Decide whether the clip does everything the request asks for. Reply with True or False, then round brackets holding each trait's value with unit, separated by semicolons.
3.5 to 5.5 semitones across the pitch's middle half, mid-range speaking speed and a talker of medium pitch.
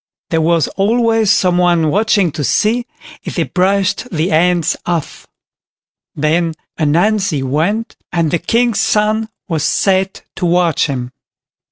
False (4.7 semitones; 130 wpm; 180 Hz)